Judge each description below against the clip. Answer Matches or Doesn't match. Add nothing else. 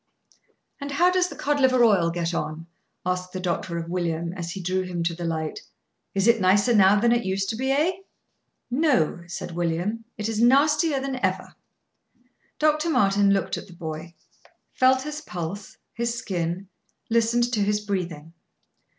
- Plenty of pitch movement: Matches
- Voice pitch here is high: Matches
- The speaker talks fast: Doesn't match